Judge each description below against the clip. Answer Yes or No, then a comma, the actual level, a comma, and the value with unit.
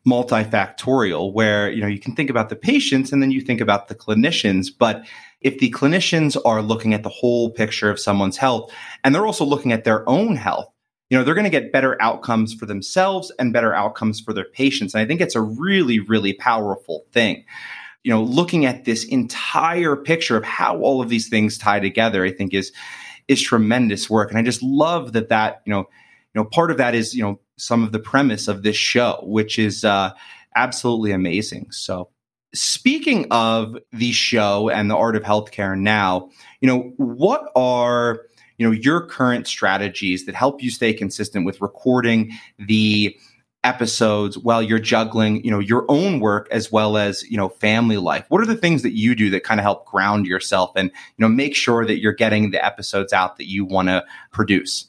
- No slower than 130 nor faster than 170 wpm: No, average, 200 wpm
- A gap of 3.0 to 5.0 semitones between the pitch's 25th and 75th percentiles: Yes, average, 3.4 semitones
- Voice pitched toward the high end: No, low, 115 Hz